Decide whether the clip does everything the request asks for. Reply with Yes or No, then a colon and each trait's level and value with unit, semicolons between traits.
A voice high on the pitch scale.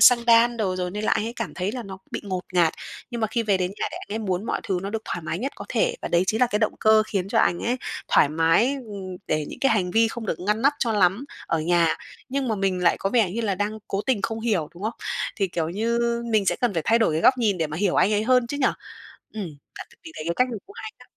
Yes: high, 210 Hz